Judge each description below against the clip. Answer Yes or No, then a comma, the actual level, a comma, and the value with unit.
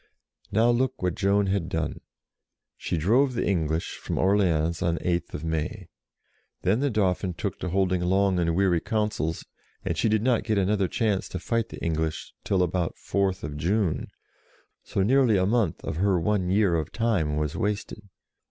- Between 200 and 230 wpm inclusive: No, average, 170 wpm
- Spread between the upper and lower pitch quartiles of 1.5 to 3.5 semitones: No, average, 4.0 semitones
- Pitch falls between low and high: No, very low, 95 Hz